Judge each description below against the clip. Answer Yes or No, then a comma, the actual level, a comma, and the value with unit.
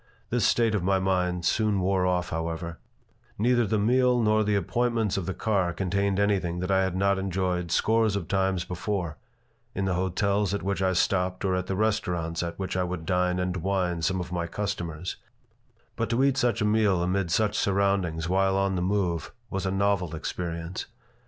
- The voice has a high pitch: No, very low, 95 Hz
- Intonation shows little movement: Yes, narrow, 2.3 semitones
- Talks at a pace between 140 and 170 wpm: No, average, 190 wpm